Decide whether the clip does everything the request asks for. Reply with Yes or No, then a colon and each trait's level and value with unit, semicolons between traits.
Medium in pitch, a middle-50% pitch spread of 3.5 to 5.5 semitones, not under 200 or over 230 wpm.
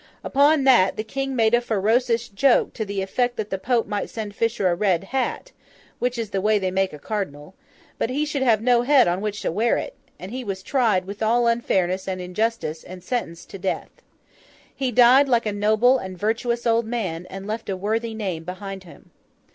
No: high, 215 Hz; average, 3.9 semitones; fast, 205 wpm